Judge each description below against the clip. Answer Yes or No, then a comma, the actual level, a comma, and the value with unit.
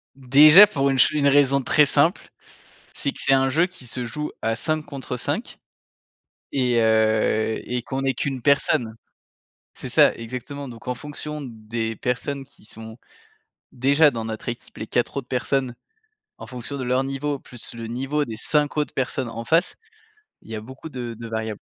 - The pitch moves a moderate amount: Yes, average, 3.4 semitones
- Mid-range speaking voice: No, low, 130 Hz